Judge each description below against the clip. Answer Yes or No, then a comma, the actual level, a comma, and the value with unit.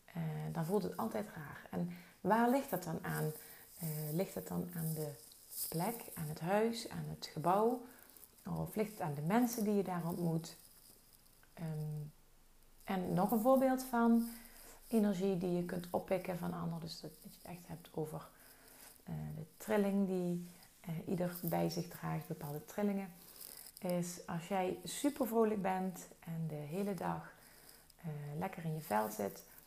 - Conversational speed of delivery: Yes, average, 165 wpm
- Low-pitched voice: No, medium, 175 Hz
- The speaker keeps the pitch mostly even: No, average, 4.3 semitones